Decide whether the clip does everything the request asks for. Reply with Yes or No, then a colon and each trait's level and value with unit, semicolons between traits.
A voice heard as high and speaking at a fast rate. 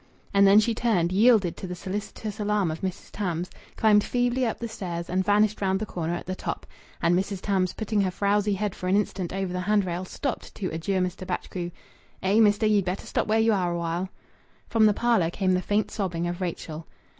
Yes: high, 195 Hz; fast, 215 wpm